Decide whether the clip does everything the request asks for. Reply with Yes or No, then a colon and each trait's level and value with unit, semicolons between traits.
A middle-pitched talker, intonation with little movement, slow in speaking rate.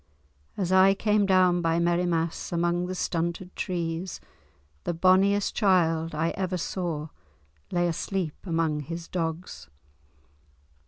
Yes: medium, 175 Hz; narrow, 2.1 semitones; slow, 115 wpm